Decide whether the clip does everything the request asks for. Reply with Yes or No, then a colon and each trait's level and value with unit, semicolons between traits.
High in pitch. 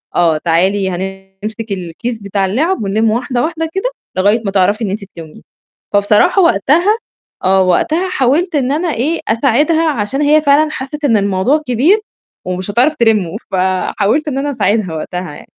Yes: high, 225 Hz